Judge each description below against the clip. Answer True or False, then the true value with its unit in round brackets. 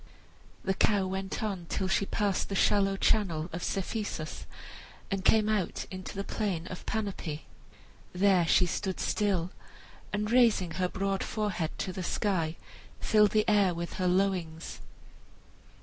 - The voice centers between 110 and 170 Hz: False (190 Hz)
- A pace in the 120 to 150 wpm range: True (145 wpm)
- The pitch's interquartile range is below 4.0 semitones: True (2.5 semitones)